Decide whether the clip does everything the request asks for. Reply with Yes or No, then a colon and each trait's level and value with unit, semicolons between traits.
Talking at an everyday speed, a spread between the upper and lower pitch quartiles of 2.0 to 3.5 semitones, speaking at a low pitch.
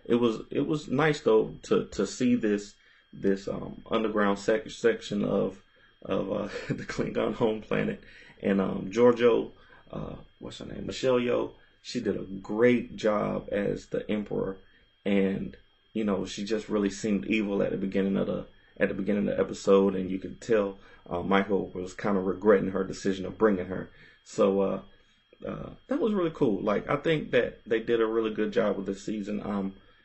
Yes: average, 190 wpm; average, 2.8 semitones; low, 105 Hz